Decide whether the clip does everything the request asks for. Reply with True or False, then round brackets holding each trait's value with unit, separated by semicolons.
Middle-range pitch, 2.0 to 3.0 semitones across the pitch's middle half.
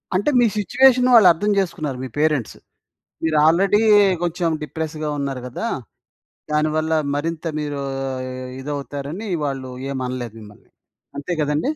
False (155 Hz; 4.0 semitones)